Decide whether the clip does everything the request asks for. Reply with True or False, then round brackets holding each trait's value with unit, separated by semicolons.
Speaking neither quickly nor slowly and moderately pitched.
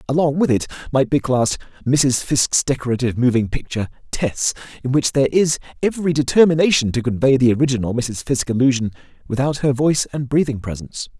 False (165 wpm; 130 Hz)